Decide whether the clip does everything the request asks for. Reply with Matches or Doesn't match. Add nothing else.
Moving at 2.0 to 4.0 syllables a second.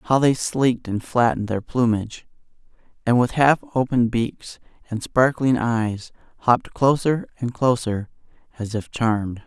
Doesn't match